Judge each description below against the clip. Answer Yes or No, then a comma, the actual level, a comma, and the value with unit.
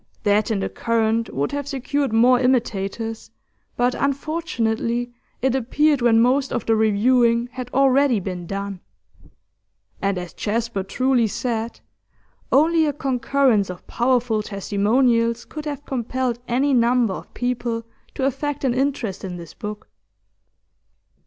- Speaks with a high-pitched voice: Yes, high, 240 Hz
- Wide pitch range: No, average, 3.4 semitones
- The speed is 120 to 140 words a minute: Yes, slow, 135 wpm